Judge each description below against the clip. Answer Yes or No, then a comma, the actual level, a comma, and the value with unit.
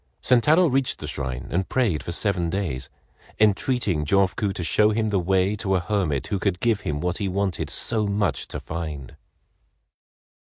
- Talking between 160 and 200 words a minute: Yes, average, 170 wpm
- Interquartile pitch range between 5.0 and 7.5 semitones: No, average, 4.1 semitones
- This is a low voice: Yes, very low, 95 Hz